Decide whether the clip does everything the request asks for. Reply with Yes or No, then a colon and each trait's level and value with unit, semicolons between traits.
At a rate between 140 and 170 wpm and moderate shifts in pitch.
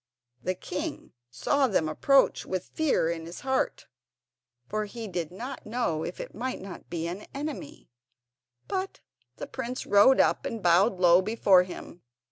No: average, 155 wpm; wide, 6.9 semitones